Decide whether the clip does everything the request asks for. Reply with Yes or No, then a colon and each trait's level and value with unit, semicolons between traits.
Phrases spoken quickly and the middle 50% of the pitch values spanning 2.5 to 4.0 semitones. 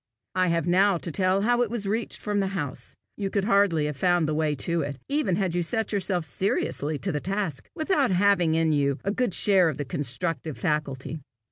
No: fast, 215 wpm; average, 4.6 semitones